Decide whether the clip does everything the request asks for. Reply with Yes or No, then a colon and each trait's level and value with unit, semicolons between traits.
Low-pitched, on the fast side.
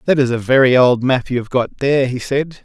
Yes: low, 130 Hz; fast, 275 wpm